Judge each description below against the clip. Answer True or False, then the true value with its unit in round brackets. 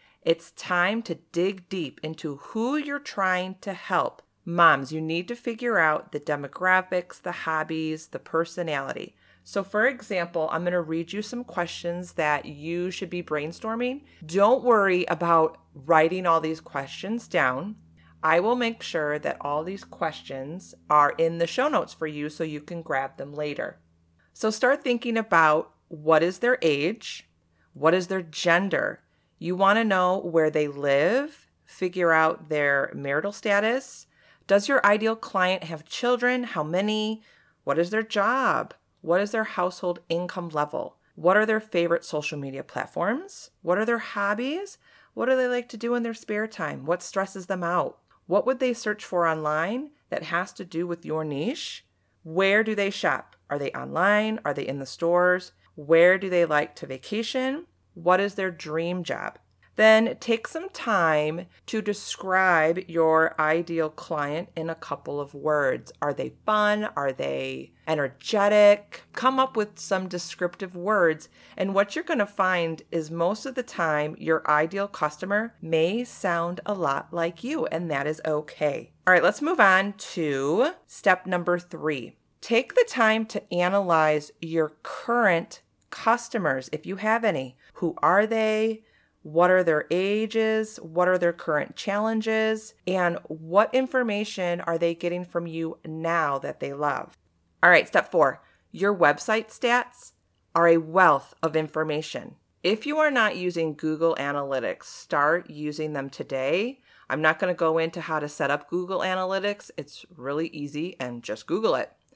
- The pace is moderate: True (165 wpm)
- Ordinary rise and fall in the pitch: True (4.9 semitones)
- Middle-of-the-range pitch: True (175 Hz)